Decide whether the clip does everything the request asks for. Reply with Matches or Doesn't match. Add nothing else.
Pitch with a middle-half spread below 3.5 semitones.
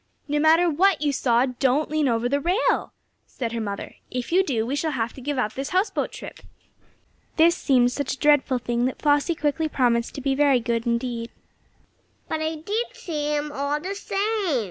Doesn't match